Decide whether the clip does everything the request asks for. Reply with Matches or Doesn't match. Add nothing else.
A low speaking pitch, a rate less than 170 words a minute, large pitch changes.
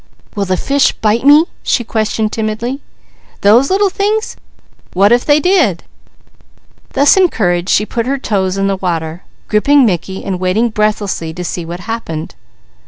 Doesn't match